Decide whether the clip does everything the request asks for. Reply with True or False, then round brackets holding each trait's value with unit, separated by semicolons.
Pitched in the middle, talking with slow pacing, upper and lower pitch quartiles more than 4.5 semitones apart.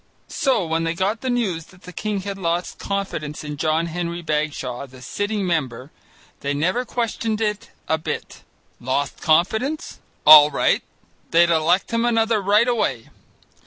False (175 Hz; 155 wpm; 5.5 semitones)